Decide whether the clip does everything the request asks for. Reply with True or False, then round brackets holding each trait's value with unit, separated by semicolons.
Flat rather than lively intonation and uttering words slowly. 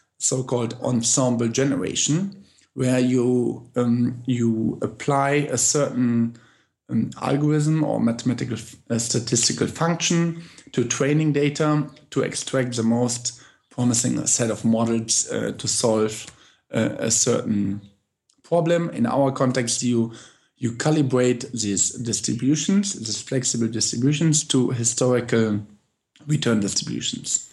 False (3.9 semitones; 115 wpm)